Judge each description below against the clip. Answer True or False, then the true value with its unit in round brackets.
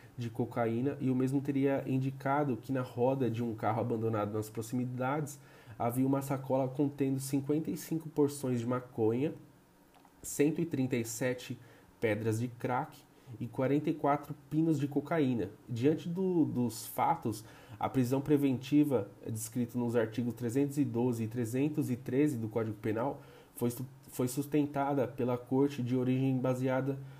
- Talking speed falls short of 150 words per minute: True (125 wpm)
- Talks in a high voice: False (130 Hz)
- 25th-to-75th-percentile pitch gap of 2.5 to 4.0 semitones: True (2.9 semitones)